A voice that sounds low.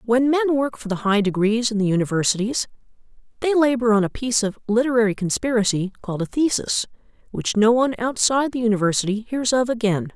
No: high, 230 Hz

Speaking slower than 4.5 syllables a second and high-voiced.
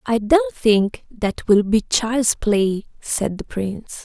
Yes: 3.2 syllables/s; high, 215 Hz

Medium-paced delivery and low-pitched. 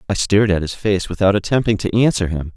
No: fast, 235 wpm; low, 100 Hz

